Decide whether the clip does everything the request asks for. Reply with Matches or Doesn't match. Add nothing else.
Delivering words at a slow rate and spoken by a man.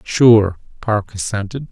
Matches